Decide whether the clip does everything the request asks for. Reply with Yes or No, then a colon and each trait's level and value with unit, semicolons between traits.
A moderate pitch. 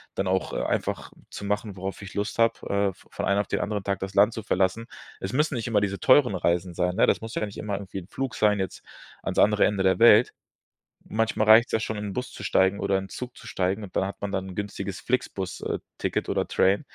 No: low, 100 Hz